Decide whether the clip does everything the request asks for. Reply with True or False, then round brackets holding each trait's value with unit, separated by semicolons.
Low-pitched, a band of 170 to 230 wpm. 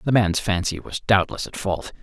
True (100 Hz; 205 wpm)